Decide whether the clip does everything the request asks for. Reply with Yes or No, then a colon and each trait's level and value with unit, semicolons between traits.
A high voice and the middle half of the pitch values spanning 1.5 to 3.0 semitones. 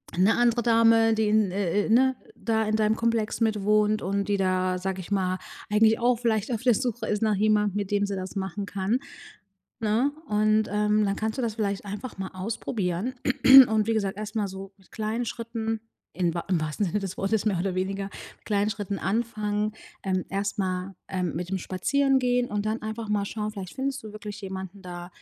Yes: high, 210 Hz; narrow, 2.4 semitones